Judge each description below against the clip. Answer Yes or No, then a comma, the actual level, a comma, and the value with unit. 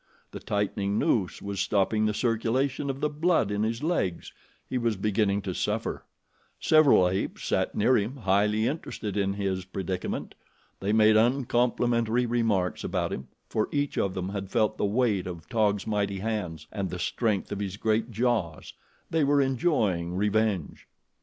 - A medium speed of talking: Yes, average, 160 wpm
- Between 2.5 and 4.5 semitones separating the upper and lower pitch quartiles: Yes, average, 3.5 semitones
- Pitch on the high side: No, low, 105 Hz